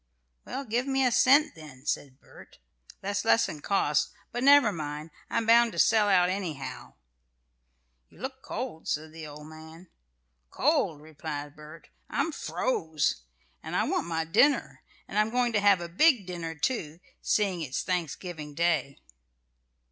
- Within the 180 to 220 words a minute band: No, average, 150 wpm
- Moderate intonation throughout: No, wide, 6.7 semitones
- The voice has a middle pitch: Yes, medium, 175 Hz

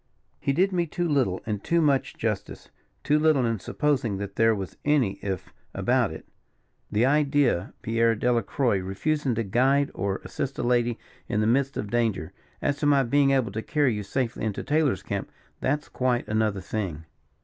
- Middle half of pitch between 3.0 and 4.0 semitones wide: No, average, 5.2 semitones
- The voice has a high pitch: No, low, 120 Hz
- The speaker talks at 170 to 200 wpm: Yes, average, 180 wpm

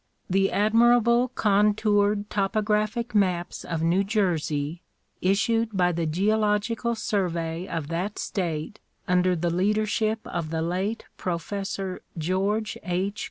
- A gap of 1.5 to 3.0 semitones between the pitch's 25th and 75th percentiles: No, average, 3.4 semitones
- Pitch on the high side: Yes, high, 195 Hz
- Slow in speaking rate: Yes, slow, 115 wpm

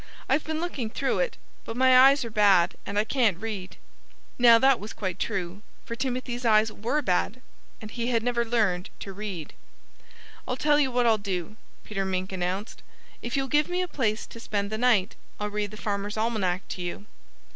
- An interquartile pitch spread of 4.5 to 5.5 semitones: No, average, 3.9 semitones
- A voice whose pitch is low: No, high, 220 Hz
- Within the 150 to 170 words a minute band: No, average, 195 wpm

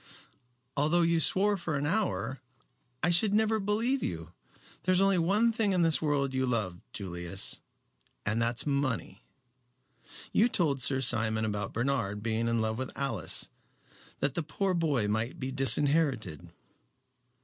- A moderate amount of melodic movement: No, wide, 7.8 semitones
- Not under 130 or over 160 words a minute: Yes, average, 150 wpm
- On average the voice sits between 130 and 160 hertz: Yes, medium, 140 Hz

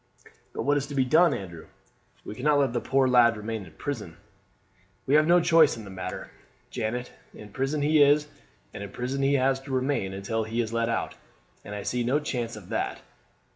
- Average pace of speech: No, fast, 210 wpm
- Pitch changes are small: No, average, 4.5 semitones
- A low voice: Yes, low, 125 Hz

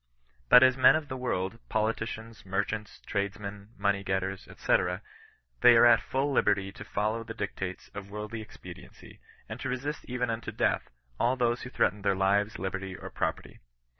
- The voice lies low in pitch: Yes, low, 105 Hz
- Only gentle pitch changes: No, average, 3.4 semitones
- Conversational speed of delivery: Yes, average, 165 wpm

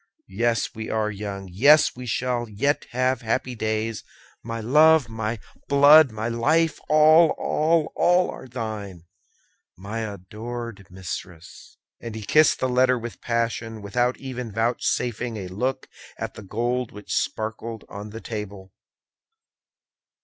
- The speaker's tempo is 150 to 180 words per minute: No, slow, 135 wpm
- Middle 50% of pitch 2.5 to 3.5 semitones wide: Yes, average, 3.1 semitones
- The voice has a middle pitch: No, low, 115 Hz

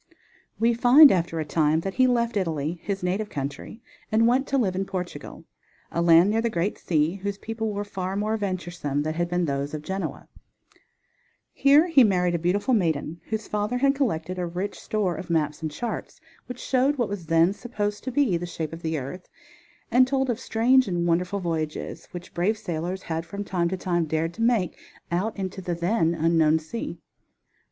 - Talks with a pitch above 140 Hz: Yes, medium, 185 Hz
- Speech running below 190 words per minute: No, average, 195 wpm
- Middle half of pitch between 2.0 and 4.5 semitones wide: No, average, 5.0 semitones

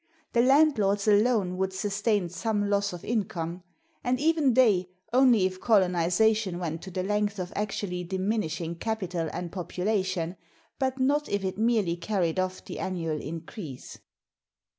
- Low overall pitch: No, high, 195 Hz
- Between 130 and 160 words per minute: Yes, average, 140 wpm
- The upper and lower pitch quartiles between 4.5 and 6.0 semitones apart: No, average, 3.6 semitones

